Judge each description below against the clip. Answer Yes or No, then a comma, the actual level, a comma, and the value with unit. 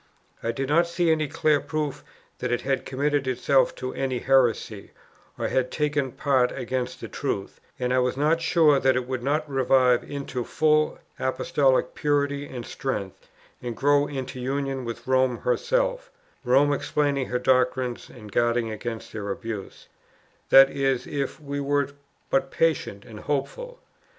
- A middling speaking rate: Yes, average, 155 wpm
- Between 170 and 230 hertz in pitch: No, low, 135 Hz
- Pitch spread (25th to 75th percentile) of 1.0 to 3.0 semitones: Yes, narrow, 2.5 semitones